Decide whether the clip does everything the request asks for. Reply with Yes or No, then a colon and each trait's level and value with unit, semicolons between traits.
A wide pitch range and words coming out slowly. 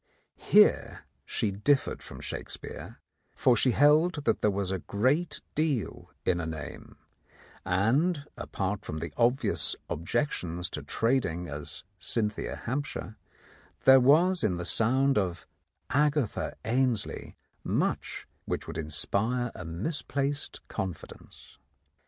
Yes: wide, 7.6 semitones; slow, 125 wpm